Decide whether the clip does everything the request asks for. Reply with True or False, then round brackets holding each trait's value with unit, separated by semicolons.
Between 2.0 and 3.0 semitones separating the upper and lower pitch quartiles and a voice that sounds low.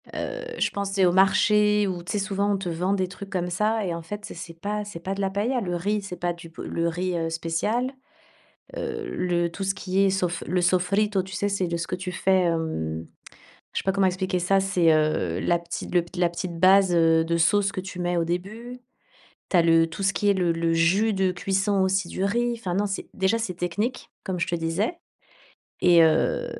False (2.7 semitones; 185 Hz)